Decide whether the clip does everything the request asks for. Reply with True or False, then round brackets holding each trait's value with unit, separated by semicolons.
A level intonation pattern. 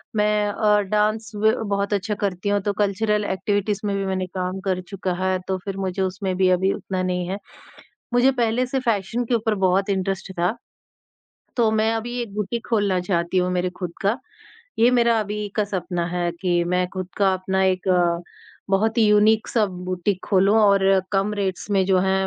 True (2.2 semitones)